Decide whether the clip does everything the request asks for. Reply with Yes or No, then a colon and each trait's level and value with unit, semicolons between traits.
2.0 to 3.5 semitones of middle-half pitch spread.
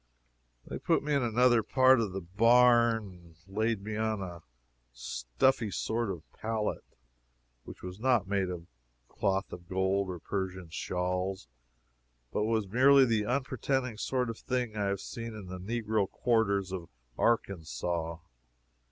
No: average, 4.1 semitones